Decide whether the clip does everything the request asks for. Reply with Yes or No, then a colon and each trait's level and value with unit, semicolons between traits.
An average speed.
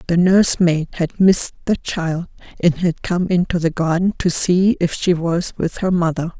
Yes: average, 190 wpm